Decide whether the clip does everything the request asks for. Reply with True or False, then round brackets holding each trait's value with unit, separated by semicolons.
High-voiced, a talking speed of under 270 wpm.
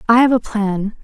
True (220 Hz; 235 wpm)